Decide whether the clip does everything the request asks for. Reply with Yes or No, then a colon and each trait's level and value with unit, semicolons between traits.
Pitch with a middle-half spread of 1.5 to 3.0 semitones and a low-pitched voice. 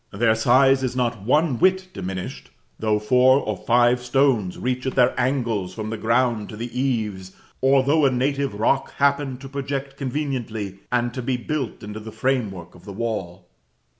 No: average, 3.8 semitones; low, 125 Hz